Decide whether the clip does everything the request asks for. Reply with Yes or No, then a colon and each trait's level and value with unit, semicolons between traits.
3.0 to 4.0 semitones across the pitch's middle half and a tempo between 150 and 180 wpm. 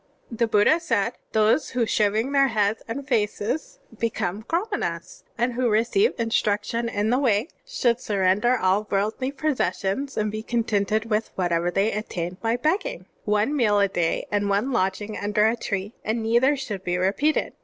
Yes: average, 3.3 semitones; average, 170 wpm